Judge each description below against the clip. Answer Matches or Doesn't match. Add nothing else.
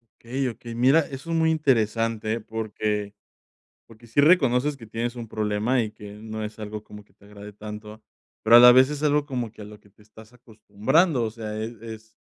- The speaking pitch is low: Matches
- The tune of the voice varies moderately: Matches